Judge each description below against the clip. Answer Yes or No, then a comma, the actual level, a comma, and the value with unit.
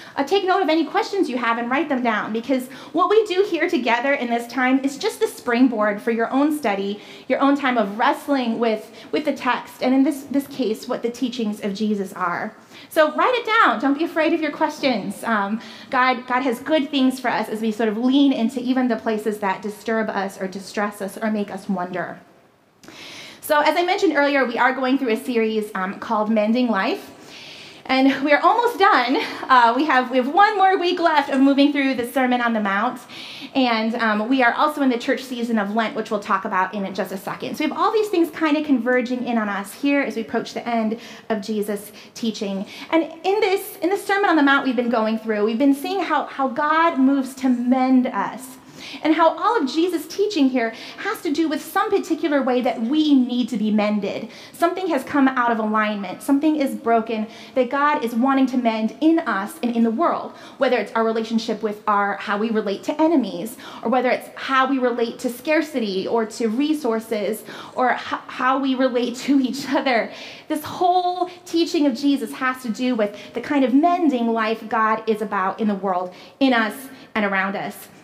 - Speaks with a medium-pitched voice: No, very high, 255 Hz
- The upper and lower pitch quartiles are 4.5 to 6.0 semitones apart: Yes, average, 4.9 semitones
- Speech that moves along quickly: Yes, fast, 215 wpm